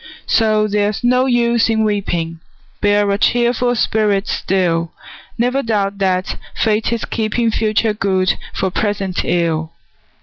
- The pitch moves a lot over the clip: No, average, 3.0 semitones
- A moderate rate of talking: No, slow, 130 wpm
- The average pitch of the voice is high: Yes, high, 210 Hz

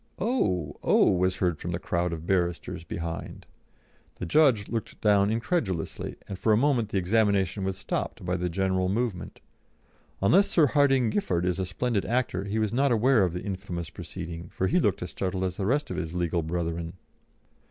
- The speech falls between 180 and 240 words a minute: Yes, average, 185 wpm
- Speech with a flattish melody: No, average, 4.3 semitones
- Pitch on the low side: Yes, very low, 95 Hz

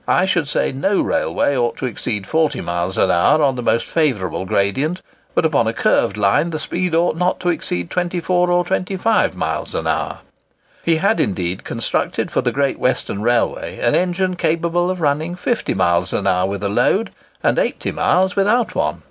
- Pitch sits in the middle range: Yes, medium, 155 Hz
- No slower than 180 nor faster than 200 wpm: Yes, average, 190 wpm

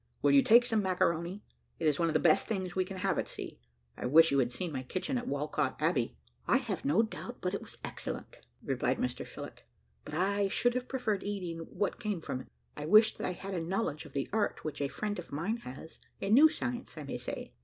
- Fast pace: Yes, fast, 240 wpm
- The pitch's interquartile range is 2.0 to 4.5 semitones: No, wide, 5.4 semitones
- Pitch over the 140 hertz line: Yes, high, 190 Hz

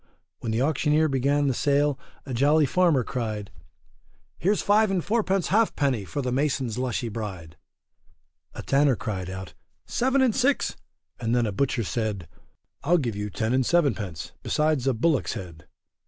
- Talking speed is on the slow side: No, average, 160 wpm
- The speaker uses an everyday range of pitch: No, wide, 6.0 semitones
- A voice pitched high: No, low, 130 Hz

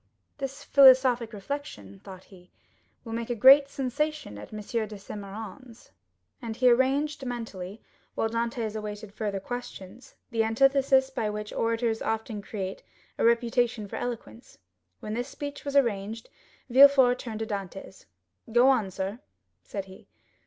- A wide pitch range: No, average, 3.8 semitones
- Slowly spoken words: No, average, 145 wpm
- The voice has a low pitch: No, high, 230 Hz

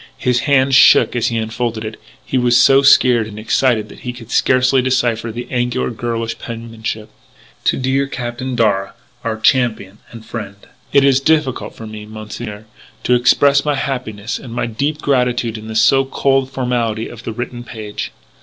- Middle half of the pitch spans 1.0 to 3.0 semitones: Yes, average, 2.7 semitones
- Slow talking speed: No, average, 175 wpm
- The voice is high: No, low, 120 Hz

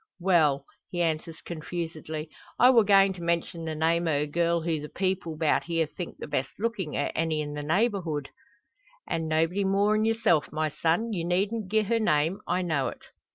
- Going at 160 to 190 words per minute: No, average, 200 wpm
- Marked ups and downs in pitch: No, average, 3.8 semitones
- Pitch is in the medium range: Yes, medium, 170 Hz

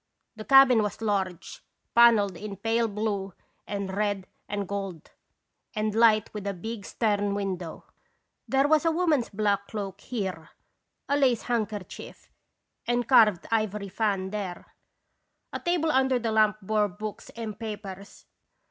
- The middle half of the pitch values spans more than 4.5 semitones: No, narrow, 2.6 semitones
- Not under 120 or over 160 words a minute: Yes, average, 140 wpm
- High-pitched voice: Yes, high, 210 Hz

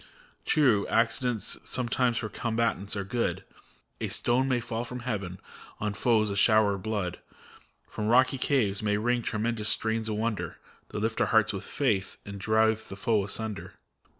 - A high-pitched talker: No, low, 110 Hz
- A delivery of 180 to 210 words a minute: No, average, 165 wpm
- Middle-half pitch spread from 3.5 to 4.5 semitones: No, narrow, 2.4 semitones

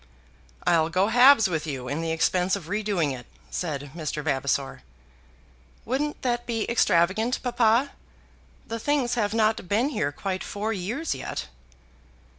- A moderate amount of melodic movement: No, wide, 6.6 semitones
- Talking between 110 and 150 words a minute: Yes, average, 140 wpm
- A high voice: Yes, high, 200 Hz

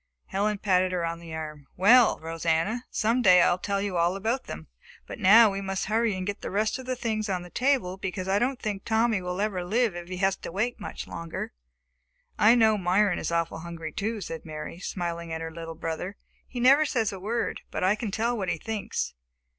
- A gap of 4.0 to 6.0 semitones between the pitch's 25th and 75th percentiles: Yes, average, 4.3 semitones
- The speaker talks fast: Yes, fast, 225 wpm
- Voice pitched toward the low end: No, high, 195 Hz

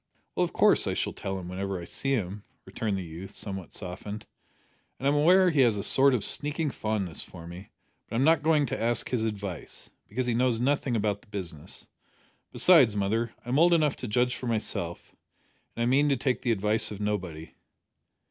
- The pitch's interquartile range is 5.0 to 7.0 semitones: Yes, average, 5.3 semitones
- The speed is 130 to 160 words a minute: No, average, 200 wpm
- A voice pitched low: Yes, low, 110 Hz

